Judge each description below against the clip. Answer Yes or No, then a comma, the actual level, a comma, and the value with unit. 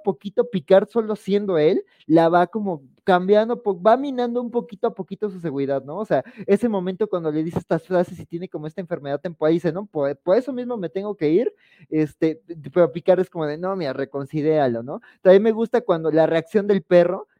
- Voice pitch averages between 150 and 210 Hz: Yes, medium, 185 Hz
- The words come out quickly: Yes, fast, 215 wpm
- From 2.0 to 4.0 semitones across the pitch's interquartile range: No, average, 4.6 semitones